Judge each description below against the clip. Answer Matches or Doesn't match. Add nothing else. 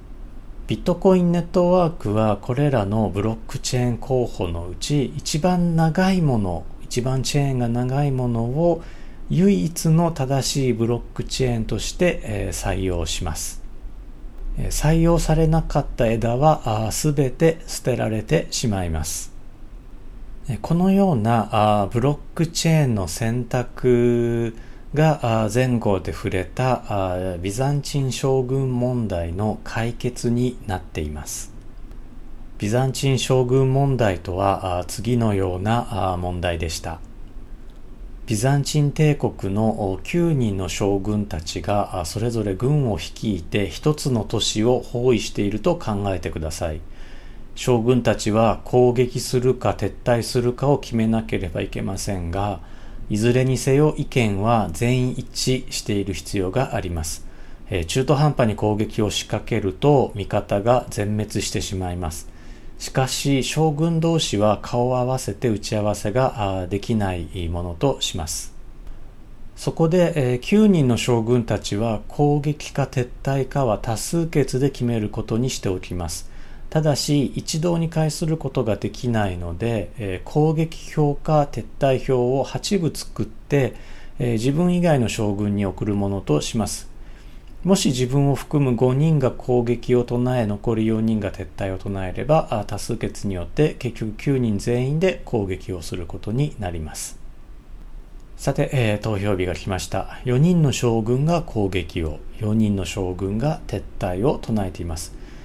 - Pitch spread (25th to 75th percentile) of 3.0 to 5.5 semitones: Matches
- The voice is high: Doesn't match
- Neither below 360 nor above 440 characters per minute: Doesn't match